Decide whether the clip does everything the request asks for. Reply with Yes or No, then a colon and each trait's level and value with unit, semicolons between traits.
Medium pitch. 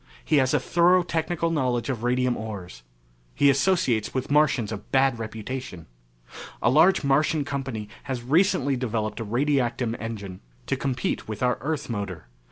No: low, 125 Hz